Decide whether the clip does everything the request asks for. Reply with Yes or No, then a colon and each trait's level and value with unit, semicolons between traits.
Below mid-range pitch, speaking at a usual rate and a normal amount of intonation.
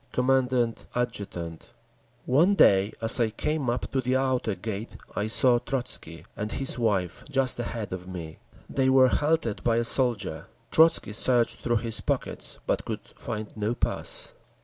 Yes: low, 120 Hz; average, 155 wpm; average, 3.7 semitones